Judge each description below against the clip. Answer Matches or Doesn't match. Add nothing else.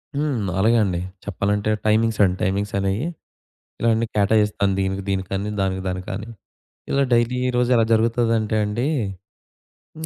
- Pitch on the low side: Matches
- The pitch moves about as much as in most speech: Matches